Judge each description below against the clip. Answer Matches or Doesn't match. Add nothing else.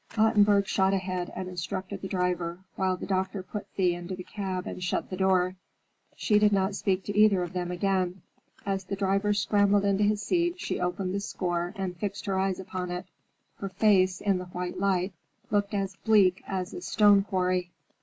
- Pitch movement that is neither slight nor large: Doesn't match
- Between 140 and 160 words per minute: Doesn't match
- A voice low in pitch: Doesn't match